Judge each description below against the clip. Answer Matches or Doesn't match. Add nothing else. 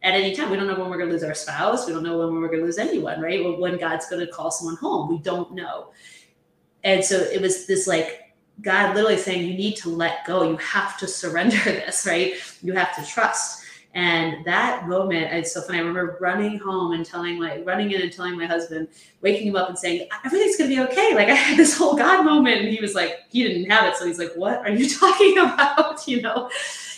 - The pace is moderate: Doesn't match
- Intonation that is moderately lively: Matches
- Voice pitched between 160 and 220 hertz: Matches